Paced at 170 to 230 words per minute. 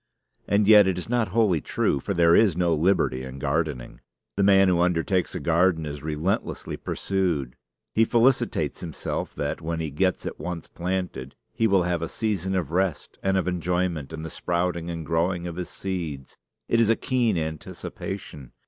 Yes: average, 180 wpm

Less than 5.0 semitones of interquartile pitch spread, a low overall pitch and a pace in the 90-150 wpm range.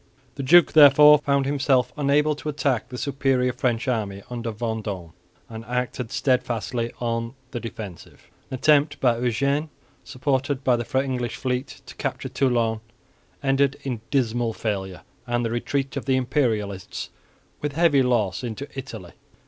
Yes: average, 3.2 semitones; low, 125 Hz; average, 145 wpm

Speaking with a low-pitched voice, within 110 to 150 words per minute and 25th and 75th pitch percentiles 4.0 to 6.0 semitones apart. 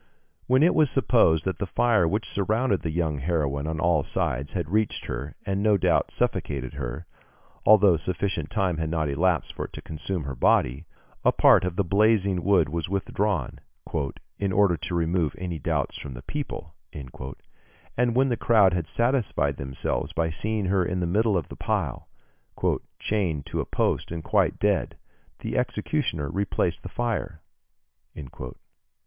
No: very low, 90 Hz; average, 165 wpm; average, 4.8 semitones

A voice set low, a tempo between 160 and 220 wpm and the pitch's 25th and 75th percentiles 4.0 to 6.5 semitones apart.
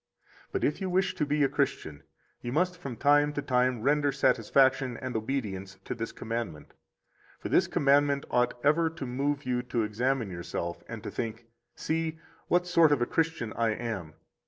Yes: low, 130 Hz; average, 180 wpm; average, 4.3 semitones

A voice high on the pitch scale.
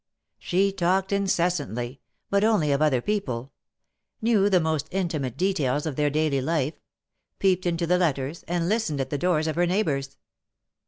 No: medium, 165 Hz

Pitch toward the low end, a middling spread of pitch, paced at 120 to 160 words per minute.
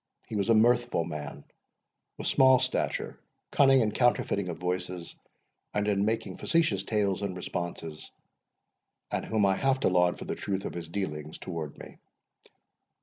Yes: low, 100 Hz; average, 4.4 semitones; average, 155 wpm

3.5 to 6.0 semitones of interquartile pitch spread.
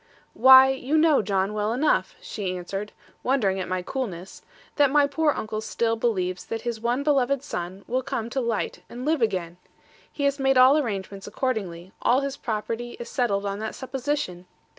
Yes: average, 5.2 semitones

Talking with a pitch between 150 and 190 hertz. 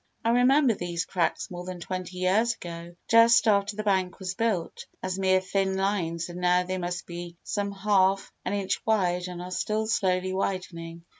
Yes: medium, 185 Hz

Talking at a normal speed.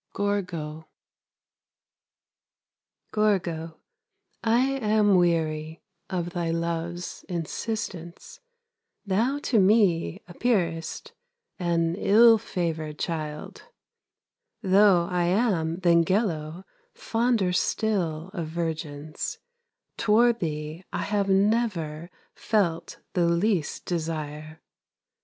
No: slow, 85 wpm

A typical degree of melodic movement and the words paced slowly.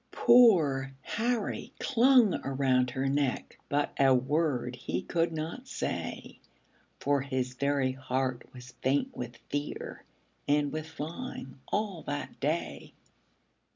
Yes: average, 4.1 semitones; slow, 120 wpm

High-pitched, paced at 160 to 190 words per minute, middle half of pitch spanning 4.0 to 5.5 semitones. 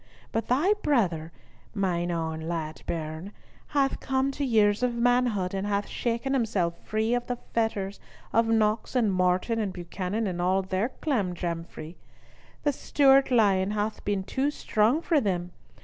No: high, 210 Hz; average, 150 wpm; average, 5.2 semitones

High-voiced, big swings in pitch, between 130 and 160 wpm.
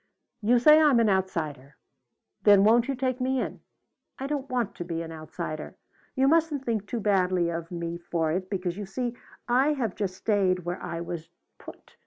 No: high, 200 Hz; wide, 6.5 semitones; average, 190 wpm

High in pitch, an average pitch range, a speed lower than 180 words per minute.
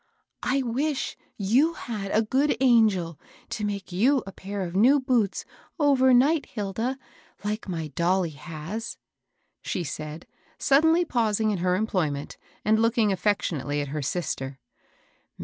No: high, 210 Hz; wide, 6.0 semitones; average, 140 wpm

